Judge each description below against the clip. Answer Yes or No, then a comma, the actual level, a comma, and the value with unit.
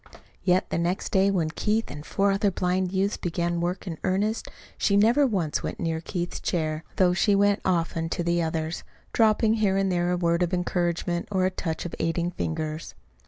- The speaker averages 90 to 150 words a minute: No, average, 195 wpm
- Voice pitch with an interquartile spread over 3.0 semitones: No, narrow, 2.6 semitones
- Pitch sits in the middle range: Yes, medium, 180 Hz